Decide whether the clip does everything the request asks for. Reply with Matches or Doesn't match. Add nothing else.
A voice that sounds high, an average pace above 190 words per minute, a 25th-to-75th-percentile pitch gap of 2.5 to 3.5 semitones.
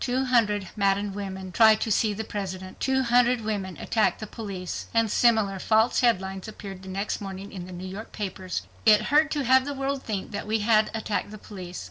Matches